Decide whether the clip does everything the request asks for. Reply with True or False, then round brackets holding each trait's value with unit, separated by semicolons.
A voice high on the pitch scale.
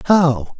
False (145 Hz)